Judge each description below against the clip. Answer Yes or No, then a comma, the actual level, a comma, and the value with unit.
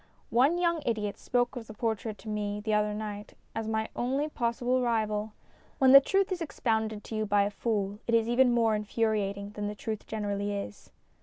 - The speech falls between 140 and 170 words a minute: No, fast, 205 wpm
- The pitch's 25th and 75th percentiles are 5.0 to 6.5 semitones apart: No, narrow, 2.6 semitones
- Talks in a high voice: Yes, high, 220 Hz